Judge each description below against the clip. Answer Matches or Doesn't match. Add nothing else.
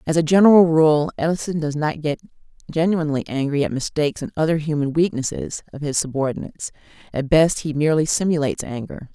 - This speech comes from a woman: Matches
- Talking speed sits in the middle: Matches